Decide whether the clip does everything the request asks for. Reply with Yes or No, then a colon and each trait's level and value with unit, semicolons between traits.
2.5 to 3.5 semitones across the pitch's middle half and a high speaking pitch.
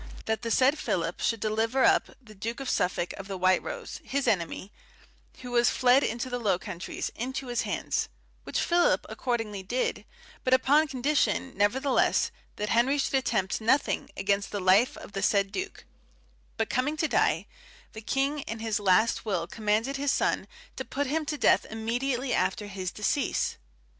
No: average, 4.6 semitones; high, 230 Hz